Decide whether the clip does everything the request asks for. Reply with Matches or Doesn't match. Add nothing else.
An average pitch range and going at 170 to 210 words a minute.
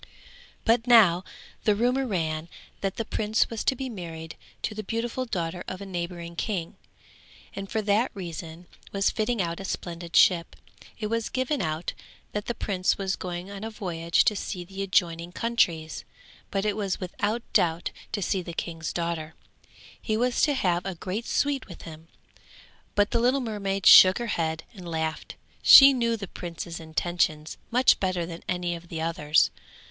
Matches